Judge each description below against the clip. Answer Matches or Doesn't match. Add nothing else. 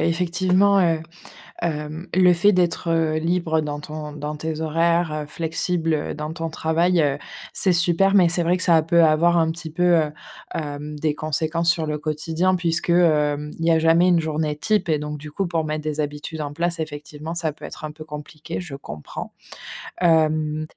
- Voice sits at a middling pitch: Matches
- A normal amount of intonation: Doesn't match